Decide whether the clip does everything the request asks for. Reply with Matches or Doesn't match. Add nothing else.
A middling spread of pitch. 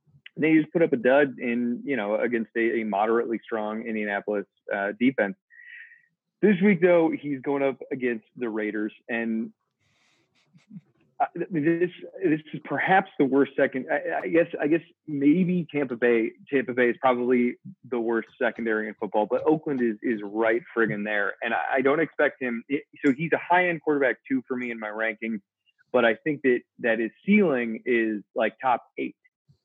Doesn't match